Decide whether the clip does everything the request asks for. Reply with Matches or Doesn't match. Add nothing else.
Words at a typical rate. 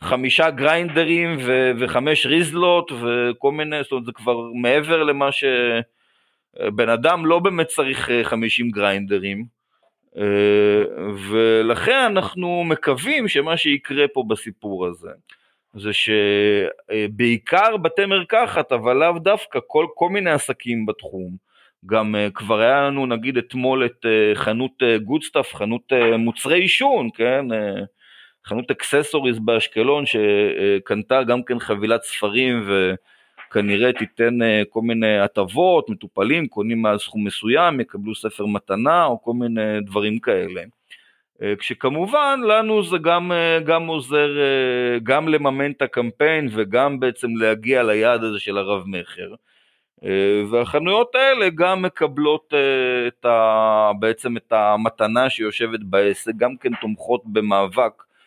Matches